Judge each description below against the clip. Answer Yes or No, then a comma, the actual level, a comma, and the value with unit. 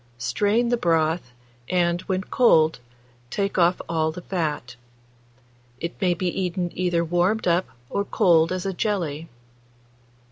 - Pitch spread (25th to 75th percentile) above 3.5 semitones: No, narrow, 2.6 semitones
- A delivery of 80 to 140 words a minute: Yes, slow, 135 wpm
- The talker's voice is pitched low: No, medium, 175 Hz